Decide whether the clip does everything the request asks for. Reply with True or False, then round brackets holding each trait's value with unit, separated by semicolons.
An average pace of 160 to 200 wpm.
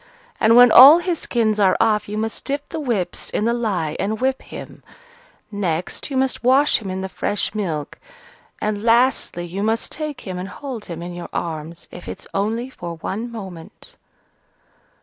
True (180 wpm)